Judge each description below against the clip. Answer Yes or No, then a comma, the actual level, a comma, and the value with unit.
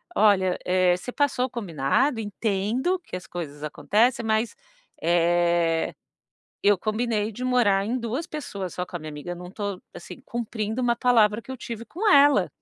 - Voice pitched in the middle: No, high, 210 Hz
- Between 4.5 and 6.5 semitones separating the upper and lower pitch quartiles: Yes, average, 5.1 semitones